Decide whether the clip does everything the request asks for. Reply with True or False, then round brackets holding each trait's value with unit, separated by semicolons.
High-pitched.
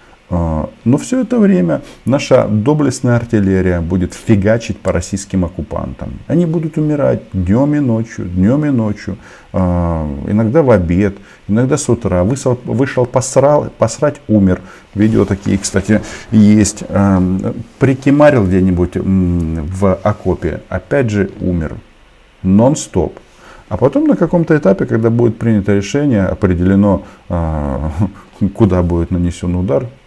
False (100 Hz)